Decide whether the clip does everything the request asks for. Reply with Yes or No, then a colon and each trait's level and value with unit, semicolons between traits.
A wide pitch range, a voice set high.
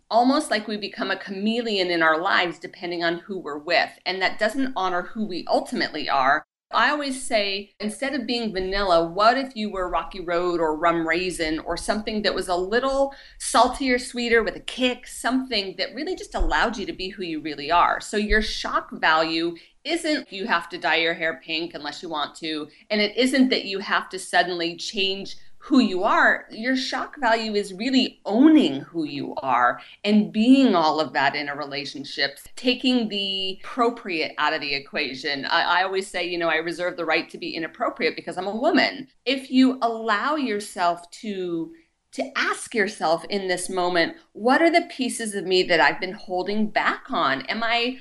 Yes: wide, 6.0 semitones; high, 200 Hz